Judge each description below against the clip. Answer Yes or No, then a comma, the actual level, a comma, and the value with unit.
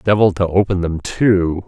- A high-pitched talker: No, very low, 95 Hz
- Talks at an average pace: Yes, average, 180 wpm